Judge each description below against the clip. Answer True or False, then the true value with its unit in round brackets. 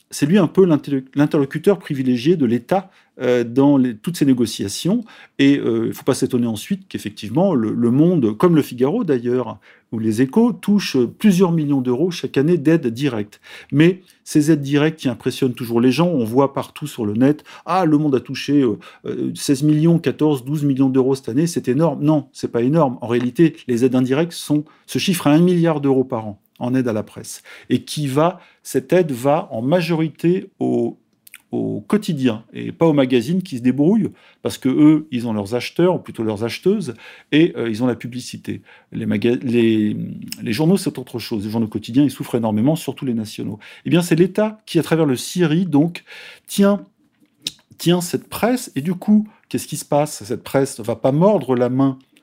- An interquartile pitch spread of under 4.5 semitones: False (5.2 semitones)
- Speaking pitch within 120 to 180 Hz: True (140 Hz)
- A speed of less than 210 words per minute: True (200 wpm)